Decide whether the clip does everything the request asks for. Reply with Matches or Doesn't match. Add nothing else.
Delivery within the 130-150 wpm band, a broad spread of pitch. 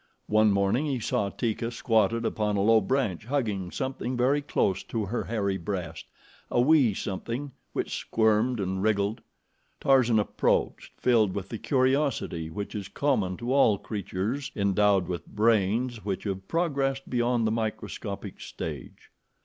Doesn't match